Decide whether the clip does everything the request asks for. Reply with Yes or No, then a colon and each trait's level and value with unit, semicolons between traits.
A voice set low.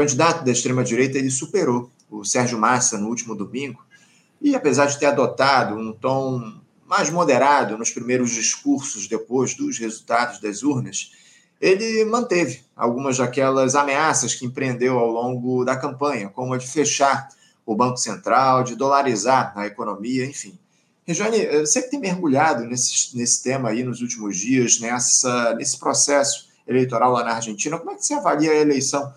Yes: low, 130 Hz